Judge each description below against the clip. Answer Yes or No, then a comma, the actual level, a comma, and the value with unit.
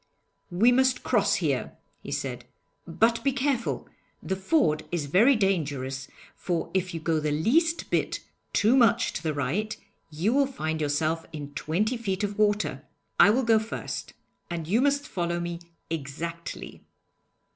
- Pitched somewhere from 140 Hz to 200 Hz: Yes, high, 190 Hz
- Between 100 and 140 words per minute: No, average, 155 wpm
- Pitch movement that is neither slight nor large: No, wide, 6.5 semitones